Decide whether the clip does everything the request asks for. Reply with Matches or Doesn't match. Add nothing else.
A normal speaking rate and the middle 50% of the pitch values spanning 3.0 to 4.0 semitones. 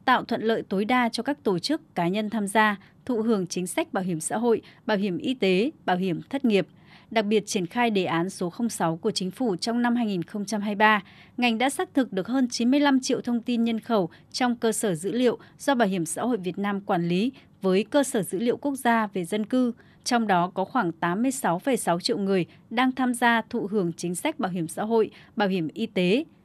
Doesn't match